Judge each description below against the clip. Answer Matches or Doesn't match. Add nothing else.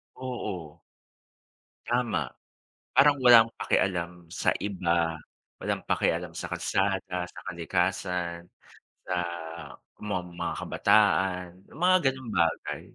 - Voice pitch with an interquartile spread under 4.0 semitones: Doesn't match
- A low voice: Matches